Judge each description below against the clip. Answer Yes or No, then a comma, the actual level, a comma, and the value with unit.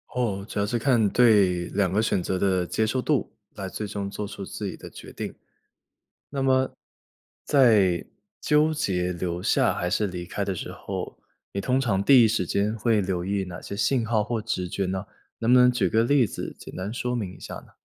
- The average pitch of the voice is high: No, low, 105 Hz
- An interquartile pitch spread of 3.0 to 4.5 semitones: Yes, average, 4.2 semitones